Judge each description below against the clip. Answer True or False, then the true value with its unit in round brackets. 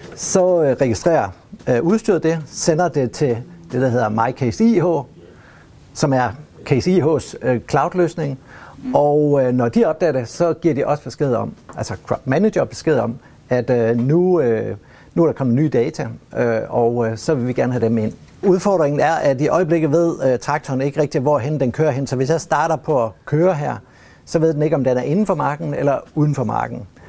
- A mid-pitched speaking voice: True (145 Hz)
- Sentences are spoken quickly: False (185 wpm)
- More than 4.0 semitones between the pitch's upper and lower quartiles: True (4.7 semitones)